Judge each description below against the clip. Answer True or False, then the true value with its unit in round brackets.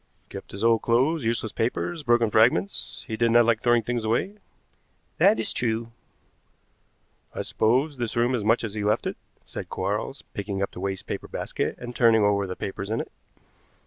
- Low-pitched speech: True (115 Hz)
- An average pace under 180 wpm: False (185 wpm)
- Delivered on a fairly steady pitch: True (2.0 semitones)